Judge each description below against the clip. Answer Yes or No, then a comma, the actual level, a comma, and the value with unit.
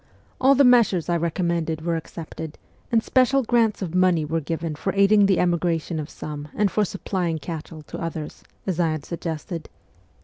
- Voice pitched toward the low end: No, medium, 170 Hz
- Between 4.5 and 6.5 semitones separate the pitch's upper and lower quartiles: No, average, 3.6 semitones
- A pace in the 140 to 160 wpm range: No, average, 175 wpm